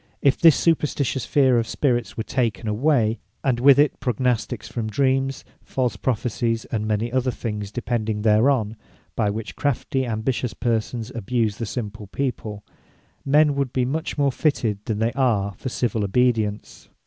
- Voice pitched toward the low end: Yes, low, 120 Hz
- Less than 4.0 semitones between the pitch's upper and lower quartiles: Yes, average, 3.5 semitones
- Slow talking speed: No, average, 155 wpm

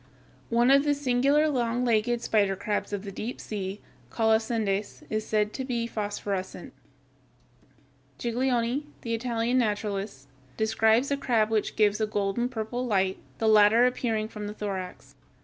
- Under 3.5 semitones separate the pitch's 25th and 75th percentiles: Yes, average, 2.7 semitones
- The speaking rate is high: No, average, 145 wpm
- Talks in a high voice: Yes, high, 220 Hz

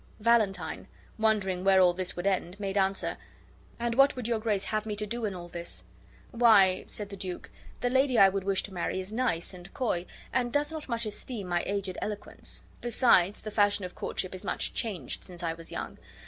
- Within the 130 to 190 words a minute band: No, fast, 205 wpm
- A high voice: Yes, high, 200 Hz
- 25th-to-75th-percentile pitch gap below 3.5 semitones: No, average, 3.8 semitones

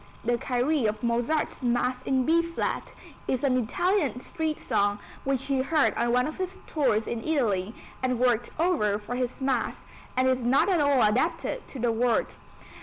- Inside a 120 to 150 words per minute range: No, average, 180 wpm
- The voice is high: Yes, very high, 255 Hz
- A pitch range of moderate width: Yes, average, 4.0 semitones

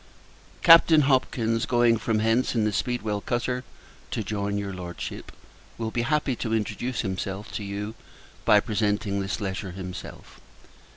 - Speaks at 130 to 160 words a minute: Yes, average, 140 wpm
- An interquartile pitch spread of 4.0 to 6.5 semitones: No, average, 3.2 semitones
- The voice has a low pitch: Yes, low, 110 Hz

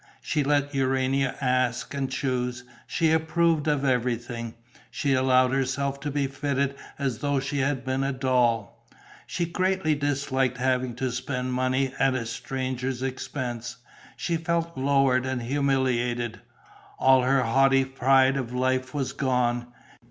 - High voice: No, low, 130 Hz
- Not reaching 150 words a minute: Yes, average, 140 wpm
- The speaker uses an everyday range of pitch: No, narrow, 1.7 semitones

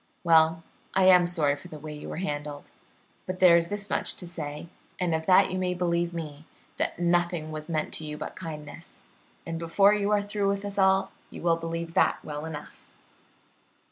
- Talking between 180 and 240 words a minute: Yes, average, 200 wpm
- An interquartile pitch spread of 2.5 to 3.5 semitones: Yes, average, 2.9 semitones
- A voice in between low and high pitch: Yes, medium, 170 Hz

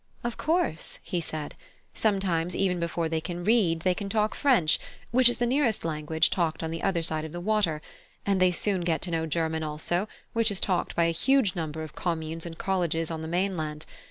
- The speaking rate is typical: No, fast, 210 wpm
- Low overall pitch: No, medium, 170 Hz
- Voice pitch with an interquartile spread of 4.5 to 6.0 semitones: No, average, 3.7 semitones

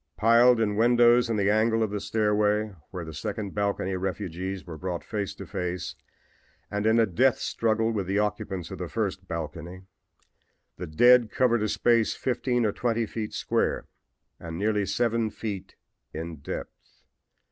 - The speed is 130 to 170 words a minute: Yes, average, 160 wpm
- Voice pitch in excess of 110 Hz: No, low, 105 Hz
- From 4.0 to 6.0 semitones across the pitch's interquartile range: No, average, 3.2 semitones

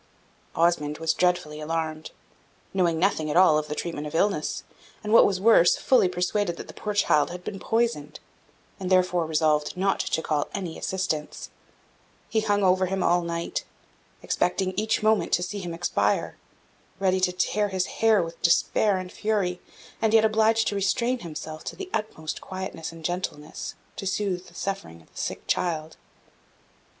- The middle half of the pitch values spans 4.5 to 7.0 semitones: No, average, 3.9 semitones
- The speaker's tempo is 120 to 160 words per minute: No, average, 170 wpm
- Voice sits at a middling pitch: Yes, medium, 180 Hz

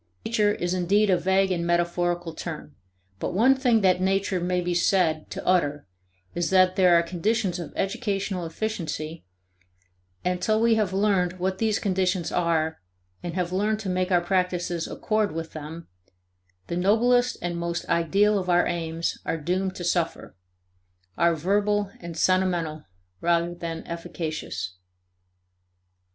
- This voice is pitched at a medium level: Yes, medium, 180 Hz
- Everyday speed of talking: Yes, average, 150 wpm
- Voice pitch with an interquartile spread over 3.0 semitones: No, narrow, 2.4 semitones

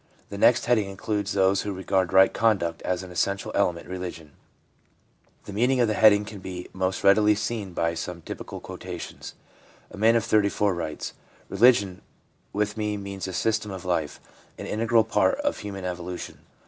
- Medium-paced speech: Yes, average, 175 wpm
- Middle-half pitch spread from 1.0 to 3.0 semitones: Yes, narrow, 2.6 semitones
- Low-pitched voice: Yes, low, 100 Hz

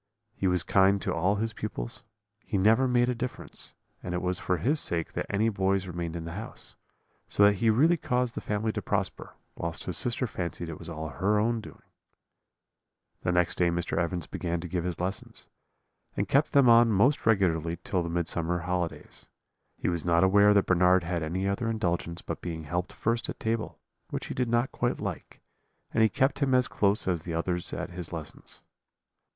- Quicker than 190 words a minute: Yes, average, 200 wpm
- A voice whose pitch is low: Yes, very low, 95 Hz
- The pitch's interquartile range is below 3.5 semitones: No, average, 4.5 semitones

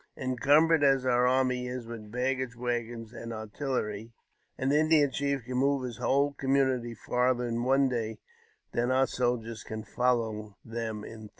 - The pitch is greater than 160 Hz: No, low, 125 Hz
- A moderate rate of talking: Yes, average, 170 wpm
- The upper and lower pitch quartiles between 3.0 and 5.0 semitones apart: No, narrow, 2.5 semitones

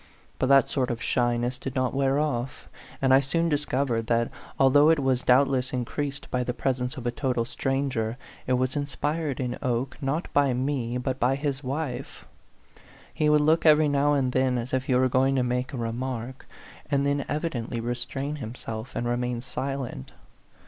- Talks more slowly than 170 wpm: No, average, 185 wpm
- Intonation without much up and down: Yes, narrow, 2.3 semitones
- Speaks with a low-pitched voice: Yes, low, 130 Hz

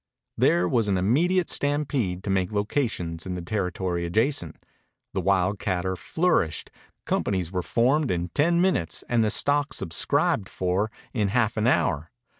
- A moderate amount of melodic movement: No, wide, 6.0 semitones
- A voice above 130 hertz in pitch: No, low, 100 Hz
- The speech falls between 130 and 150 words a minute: Yes, average, 145 wpm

